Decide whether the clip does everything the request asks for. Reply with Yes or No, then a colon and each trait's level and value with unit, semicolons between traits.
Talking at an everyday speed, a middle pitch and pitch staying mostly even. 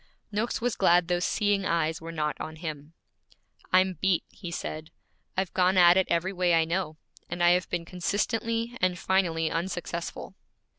Yes: average, 165 wpm; medium, 175 Hz; narrow, 2.3 semitones